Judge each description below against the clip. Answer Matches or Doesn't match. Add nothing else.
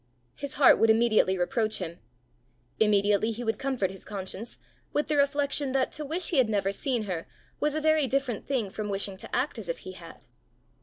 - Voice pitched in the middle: Doesn't match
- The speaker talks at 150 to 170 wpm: Doesn't match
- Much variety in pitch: Matches